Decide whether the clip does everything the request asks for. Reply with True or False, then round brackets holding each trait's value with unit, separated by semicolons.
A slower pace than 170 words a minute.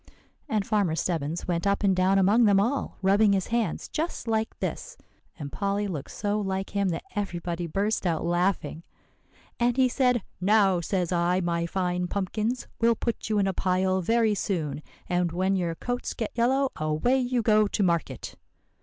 False (175 wpm)